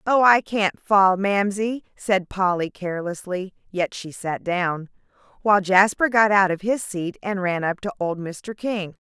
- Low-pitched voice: No, high, 195 Hz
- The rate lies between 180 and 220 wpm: No, average, 170 wpm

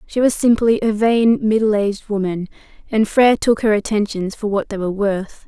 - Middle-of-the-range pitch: No, high, 210 Hz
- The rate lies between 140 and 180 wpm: No, average, 195 wpm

